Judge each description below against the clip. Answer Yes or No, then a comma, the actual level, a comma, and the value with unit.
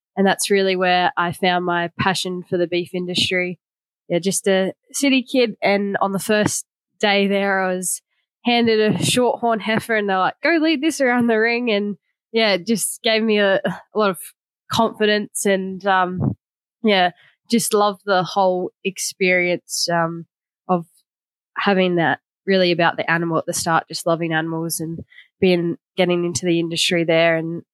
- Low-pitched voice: No, high, 190 Hz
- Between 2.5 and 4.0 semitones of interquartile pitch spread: Yes, average, 3.4 semitones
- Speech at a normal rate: Yes, average, 170 wpm